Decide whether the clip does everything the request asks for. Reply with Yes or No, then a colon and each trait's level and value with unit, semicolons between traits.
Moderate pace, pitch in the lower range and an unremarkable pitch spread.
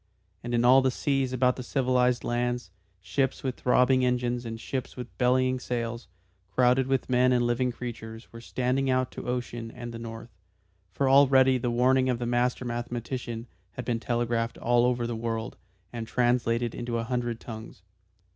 No: average, 175 wpm; low, 125 Hz; narrow, 1.3 semitones